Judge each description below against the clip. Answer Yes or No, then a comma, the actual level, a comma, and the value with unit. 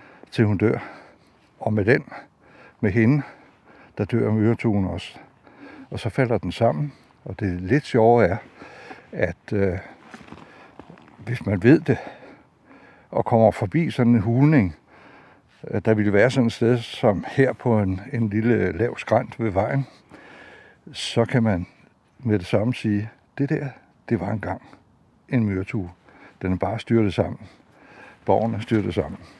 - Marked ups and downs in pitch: No, narrow, 2.6 semitones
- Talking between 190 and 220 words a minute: No, average, 150 wpm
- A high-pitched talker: No, low, 115 Hz